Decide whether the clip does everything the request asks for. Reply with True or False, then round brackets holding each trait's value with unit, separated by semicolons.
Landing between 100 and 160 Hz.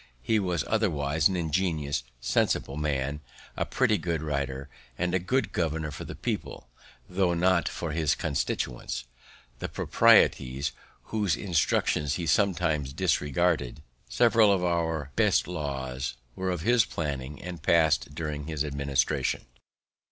False (80 Hz)